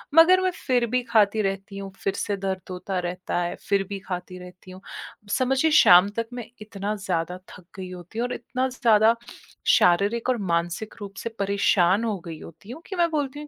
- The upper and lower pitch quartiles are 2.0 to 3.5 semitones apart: No, average, 4.8 semitones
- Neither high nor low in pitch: No, high, 200 Hz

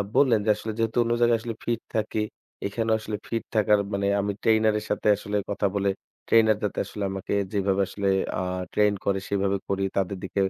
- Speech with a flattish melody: Yes, narrow, 2.0 semitones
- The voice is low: Yes, low, 105 Hz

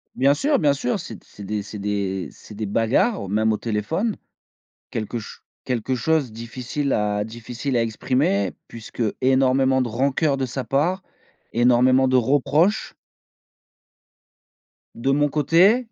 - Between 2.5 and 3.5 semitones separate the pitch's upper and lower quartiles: No, average, 4.3 semitones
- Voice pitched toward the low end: Yes, low, 125 Hz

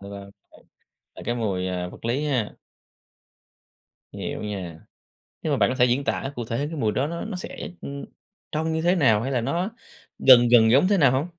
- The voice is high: No, low, 130 Hz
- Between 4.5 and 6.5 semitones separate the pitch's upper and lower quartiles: Yes, average, 5.2 semitones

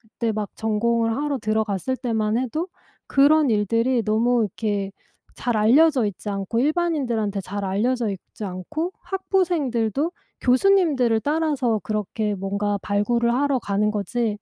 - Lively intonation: No, average, 4.7 semitones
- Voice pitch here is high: Yes, high, 230 Hz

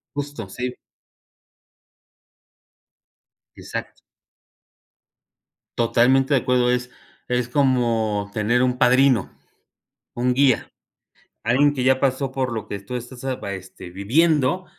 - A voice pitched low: Yes, low, 125 Hz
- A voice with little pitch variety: Yes, narrow, 2.3 semitones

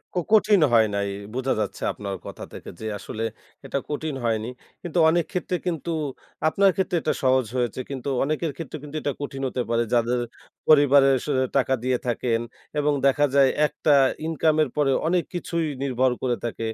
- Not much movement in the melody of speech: No, average, 4.3 semitones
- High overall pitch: No, medium, 140 Hz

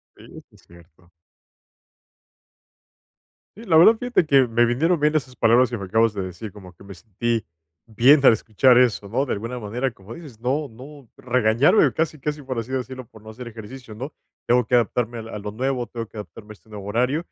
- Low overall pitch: Yes, low, 120 Hz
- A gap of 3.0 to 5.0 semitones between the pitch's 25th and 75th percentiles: Yes, average, 3.6 semitones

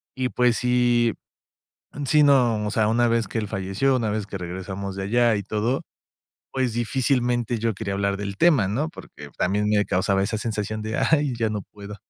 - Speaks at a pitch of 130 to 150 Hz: No, low, 110 Hz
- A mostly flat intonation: No, average, 3.3 semitones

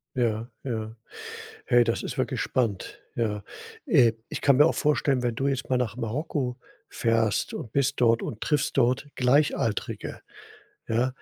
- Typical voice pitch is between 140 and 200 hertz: No, low, 125 Hz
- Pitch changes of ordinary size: Yes, average, 3.0 semitones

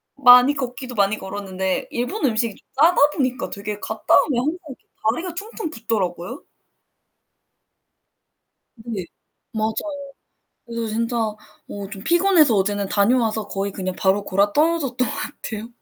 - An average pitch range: Yes, average, 4.6 semitones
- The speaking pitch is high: Yes, high, 230 Hz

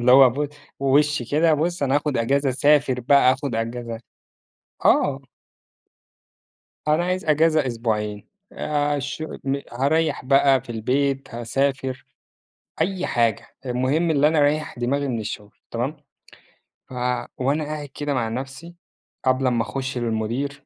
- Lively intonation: No, average, 3.2 semitones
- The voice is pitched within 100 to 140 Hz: Yes, low, 135 Hz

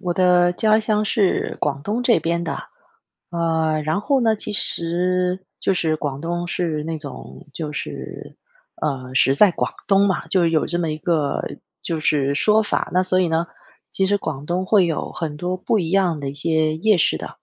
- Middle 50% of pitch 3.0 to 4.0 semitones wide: Yes, average, 3.4 semitones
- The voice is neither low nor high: Yes, medium, 175 Hz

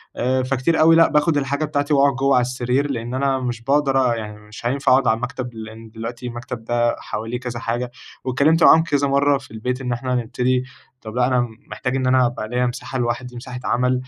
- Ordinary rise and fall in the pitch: No, narrow, 2.3 semitones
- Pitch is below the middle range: Yes, low, 125 Hz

